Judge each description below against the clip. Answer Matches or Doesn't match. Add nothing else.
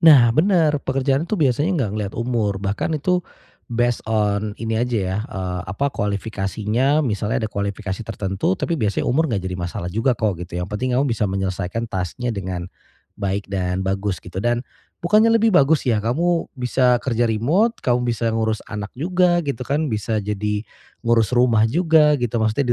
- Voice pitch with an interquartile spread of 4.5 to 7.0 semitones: Matches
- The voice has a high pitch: Doesn't match